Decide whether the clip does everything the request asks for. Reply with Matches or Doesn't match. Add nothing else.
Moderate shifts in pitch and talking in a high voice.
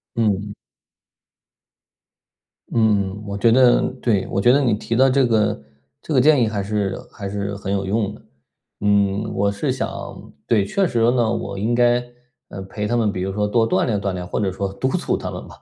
Doesn't match